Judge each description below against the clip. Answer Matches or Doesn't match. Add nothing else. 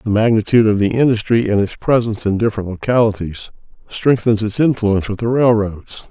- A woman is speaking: Doesn't match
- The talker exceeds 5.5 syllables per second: Matches